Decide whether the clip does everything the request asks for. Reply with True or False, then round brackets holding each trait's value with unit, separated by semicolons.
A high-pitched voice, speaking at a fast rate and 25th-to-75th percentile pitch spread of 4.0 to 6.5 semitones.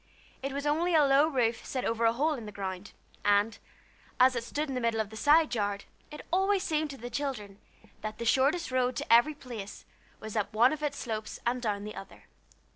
True (245 Hz; 220 wpm; 5.1 semitones)